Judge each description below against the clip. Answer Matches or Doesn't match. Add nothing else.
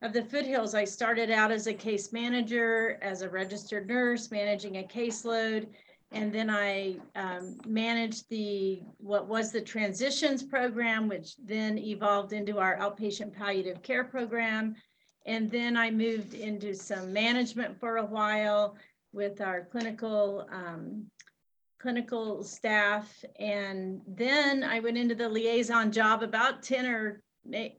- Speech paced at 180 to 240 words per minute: Doesn't match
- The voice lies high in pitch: Matches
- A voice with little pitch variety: Matches